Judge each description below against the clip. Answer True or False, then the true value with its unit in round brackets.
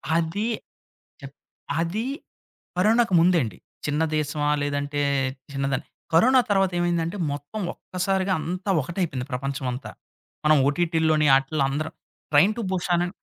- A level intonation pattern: False (4.3 semitones)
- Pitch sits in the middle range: True (165 Hz)